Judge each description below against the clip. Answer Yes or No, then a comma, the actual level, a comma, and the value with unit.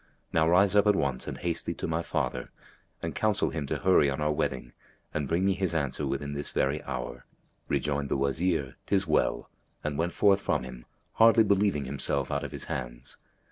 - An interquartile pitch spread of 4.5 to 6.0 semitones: Yes, average, 5.2 semitones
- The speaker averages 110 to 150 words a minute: No, average, 200 wpm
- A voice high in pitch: No, very low, 75 Hz